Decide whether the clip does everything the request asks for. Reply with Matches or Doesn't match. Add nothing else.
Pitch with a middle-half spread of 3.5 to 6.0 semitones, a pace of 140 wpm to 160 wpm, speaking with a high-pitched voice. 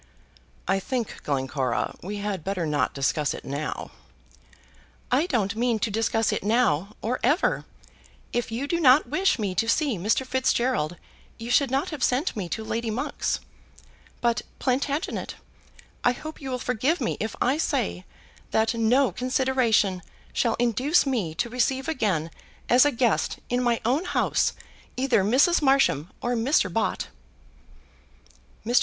Matches